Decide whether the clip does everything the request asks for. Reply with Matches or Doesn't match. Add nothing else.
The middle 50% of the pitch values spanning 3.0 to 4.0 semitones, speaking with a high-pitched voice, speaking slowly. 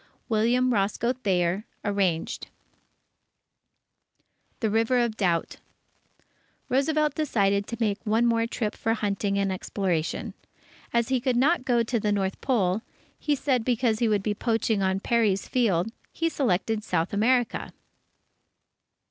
Matches